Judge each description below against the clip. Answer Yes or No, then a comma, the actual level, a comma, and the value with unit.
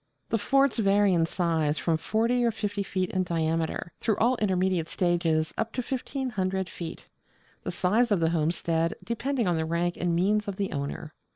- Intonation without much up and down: No, average, 4.6 semitones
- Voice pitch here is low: No, medium, 185 Hz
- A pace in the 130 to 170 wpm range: No, average, 180 wpm